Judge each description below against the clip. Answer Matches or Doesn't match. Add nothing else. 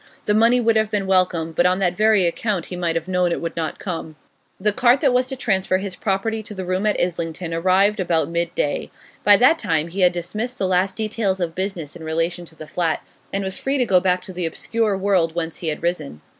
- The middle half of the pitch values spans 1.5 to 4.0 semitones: Matches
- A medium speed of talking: Doesn't match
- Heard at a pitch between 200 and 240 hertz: Doesn't match